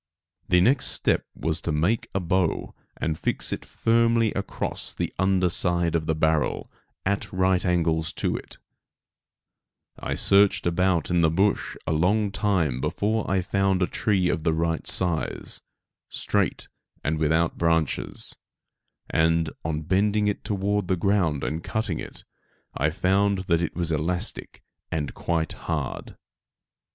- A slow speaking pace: No, average, 145 wpm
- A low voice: Yes, very low, 90 Hz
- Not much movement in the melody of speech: No, average, 3.4 semitones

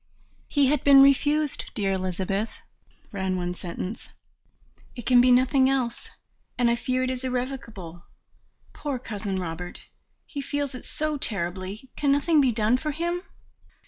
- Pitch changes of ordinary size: No, wide, 6.1 semitones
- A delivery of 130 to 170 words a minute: Yes, average, 145 wpm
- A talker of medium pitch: No, very high, 250 Hz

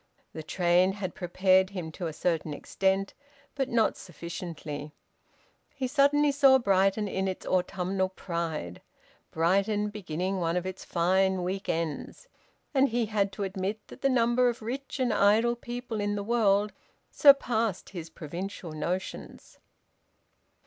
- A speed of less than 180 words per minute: Yes, average, 140 wpm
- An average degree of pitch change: Yes, average, 4.2 semitones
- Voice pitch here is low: No, high, 195 Hz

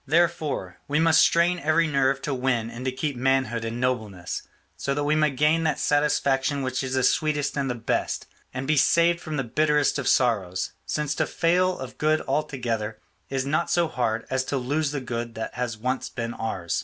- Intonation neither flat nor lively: Yes, average, 3.9 semitones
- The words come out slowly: No, average, 200 wpm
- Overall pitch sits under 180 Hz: Yes, low, 135 Hz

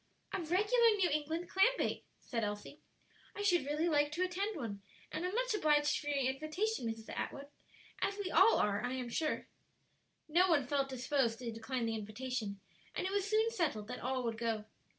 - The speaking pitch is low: No, very high, 295 Hz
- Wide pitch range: Yes, wide, 7.4 semitones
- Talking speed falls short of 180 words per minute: No, average, 190 wpm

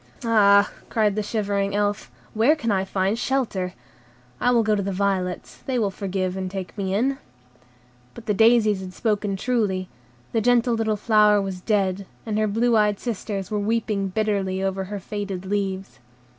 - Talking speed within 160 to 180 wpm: Yes, average, 170 wpm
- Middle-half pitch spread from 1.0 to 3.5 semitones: Yes, narrow, 2.4 semitones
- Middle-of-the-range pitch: No, high, 205 Hz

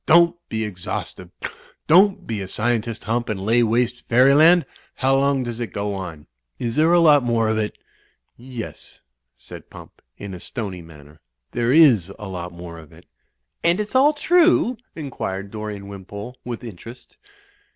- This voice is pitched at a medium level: No, low, 115 Hz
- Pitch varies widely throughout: Yes, wide, 5.7 semitones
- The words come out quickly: No, average, 160 wpm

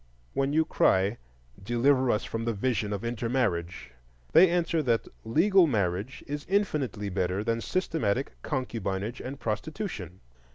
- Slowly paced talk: Yes, slow, 130 wpm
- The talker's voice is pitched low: Yes, low, 120 Hz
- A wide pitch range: Yes, wide, 6.3 semitones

